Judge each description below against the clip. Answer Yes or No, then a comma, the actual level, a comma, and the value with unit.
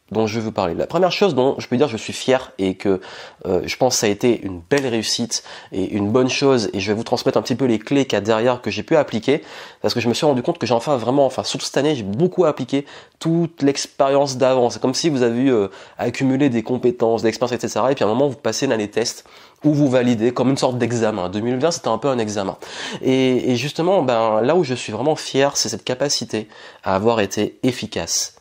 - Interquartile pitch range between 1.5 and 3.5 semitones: No, average, 3.9 semitones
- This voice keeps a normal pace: No, fast, 260 wpm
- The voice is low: Yes, low, 125 Hz